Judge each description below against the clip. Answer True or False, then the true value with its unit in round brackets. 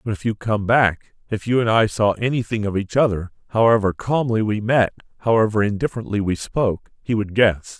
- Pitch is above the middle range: False (110 Hz)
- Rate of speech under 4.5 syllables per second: False (5.5 syllables/s)